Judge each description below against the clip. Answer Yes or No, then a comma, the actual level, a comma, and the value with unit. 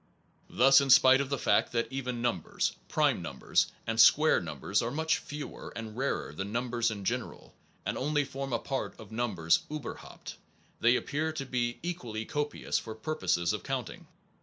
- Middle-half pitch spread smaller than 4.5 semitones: Yes, average, 4.0 semitones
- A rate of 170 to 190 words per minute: Yes, average, 175 wpm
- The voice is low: Yes, low, 125 Hz